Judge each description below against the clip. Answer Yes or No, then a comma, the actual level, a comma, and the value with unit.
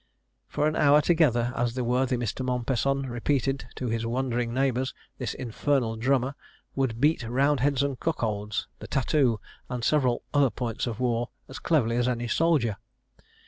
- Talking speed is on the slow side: No, average, 160 wpm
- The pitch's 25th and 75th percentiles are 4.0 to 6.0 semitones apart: No, narrow, 2.6 semitones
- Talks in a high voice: No, low, 125 Hz